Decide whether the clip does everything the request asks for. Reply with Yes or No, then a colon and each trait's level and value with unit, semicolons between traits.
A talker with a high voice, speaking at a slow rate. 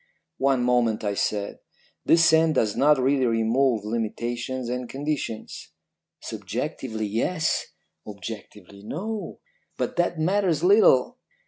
No: low, 125 Hz; slow, 110 wpm